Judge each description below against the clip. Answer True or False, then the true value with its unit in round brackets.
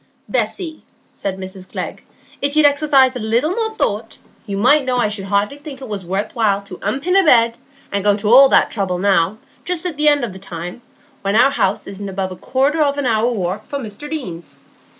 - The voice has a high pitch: True (225 Hz)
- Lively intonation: True (6.3 semitones)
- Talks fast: True (215 wpm)